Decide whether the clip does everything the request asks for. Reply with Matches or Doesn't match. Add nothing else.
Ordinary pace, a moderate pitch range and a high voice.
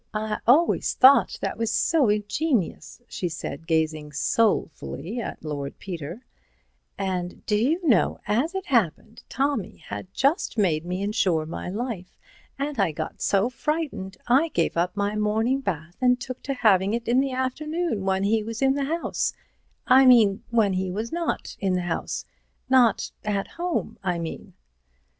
Doesn't match